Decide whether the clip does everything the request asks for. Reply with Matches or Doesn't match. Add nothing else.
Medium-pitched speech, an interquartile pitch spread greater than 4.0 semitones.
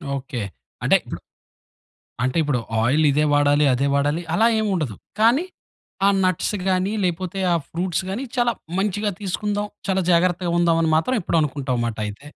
Matches